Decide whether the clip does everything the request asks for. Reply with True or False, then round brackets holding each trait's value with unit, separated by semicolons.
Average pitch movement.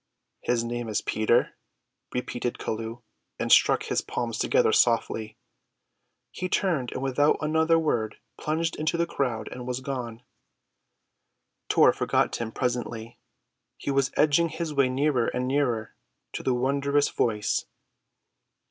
True (3.8 semitones)